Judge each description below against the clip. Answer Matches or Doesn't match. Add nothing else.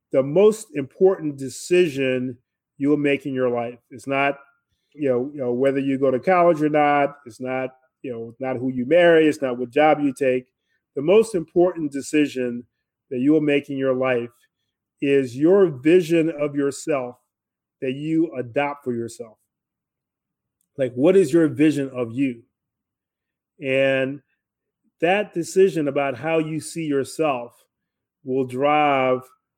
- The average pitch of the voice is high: Doesn't match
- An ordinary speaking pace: Matches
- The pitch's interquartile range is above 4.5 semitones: Doesn't match